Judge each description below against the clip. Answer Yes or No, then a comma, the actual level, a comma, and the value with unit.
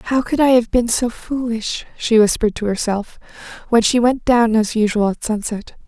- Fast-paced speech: No, average, 195 wpm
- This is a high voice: Yes, high, 230 Hz